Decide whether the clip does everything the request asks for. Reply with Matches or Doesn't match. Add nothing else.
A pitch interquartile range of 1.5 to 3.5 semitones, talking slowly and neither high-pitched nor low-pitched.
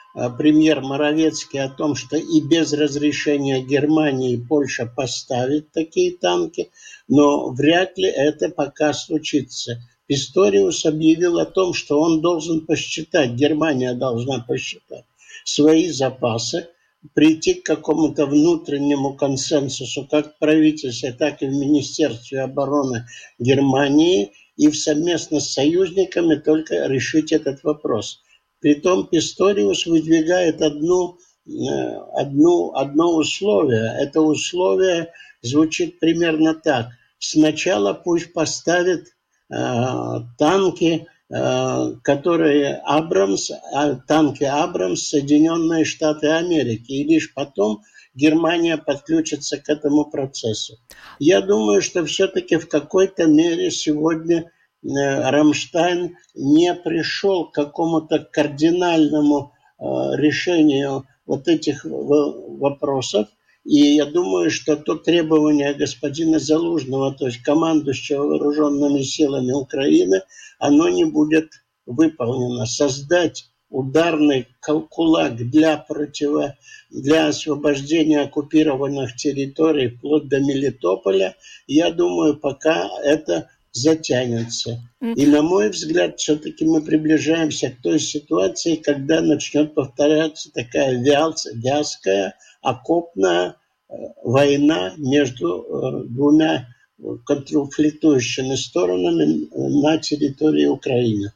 Matches